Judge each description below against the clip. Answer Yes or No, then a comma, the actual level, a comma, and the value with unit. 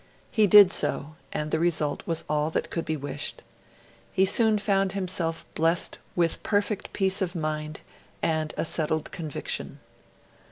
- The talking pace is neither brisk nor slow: Yes, average, 150 wpm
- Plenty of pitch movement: No, average, 3.8 semitones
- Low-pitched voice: No, medium, 165 Hz